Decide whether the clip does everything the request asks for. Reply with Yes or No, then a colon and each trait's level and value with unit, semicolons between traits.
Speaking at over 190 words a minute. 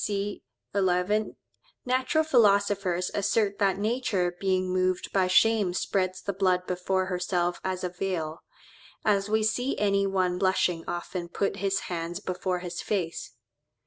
No: average, 140 wpm